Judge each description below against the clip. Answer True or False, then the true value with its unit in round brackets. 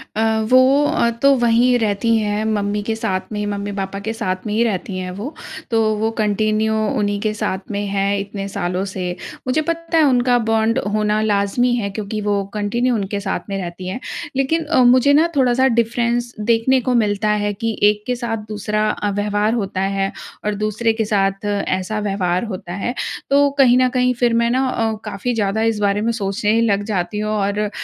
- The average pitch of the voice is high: True (215 Hz)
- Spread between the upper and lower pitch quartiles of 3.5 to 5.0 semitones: False (2.9 semitones)